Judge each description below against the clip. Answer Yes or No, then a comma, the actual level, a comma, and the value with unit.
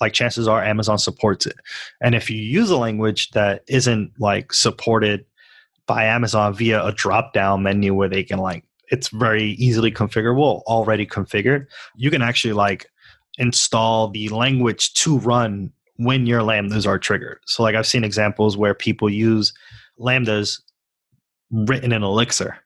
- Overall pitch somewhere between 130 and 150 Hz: No, low, 110 Hz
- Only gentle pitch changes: Yes, narrow, 2.3 semitones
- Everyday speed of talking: Yes, average, 155 wpm